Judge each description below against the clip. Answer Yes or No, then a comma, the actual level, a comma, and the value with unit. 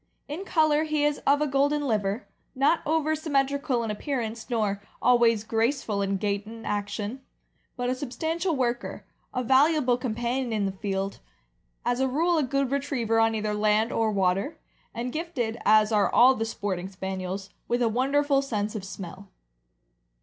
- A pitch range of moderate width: Yes, average, 5.0 semitones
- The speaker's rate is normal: Yes, average, 165 wpm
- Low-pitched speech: No, high, 240 Hz